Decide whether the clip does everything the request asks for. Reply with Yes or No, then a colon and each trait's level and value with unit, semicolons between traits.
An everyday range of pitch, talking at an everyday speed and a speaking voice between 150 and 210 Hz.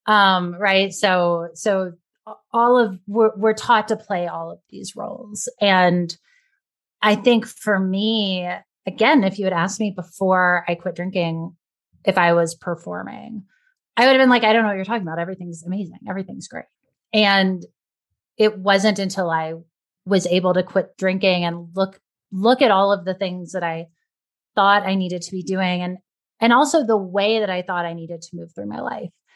Yes: average, 3.2 semitones; average, 185 wpm; high, 190 Hz